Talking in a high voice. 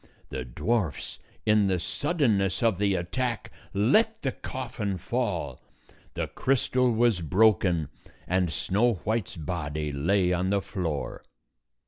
No: low, 100 Hz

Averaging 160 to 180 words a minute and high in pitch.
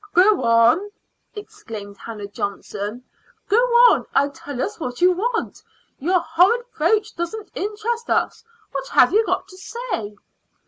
No: average, 140 wpm; very high, 365 Hz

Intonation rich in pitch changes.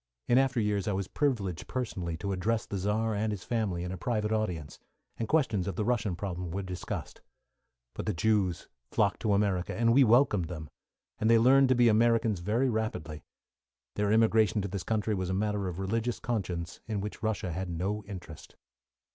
No: average, 3.4 semitones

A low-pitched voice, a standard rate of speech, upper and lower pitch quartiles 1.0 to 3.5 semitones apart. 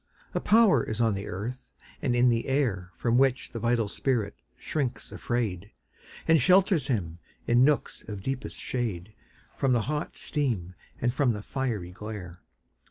No: low, 120 Hz; average, 160 wpm; average, 4.5 semitones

